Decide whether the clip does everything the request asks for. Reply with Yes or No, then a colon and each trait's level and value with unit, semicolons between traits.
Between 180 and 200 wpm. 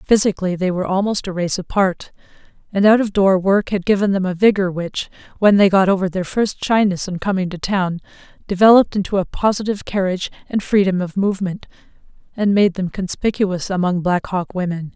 Yes: average, 185 wpm